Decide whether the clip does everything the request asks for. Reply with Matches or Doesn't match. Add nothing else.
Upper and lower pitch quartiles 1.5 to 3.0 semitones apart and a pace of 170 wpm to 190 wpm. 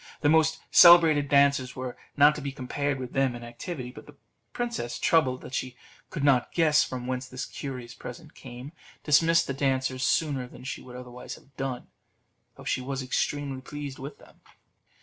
Matches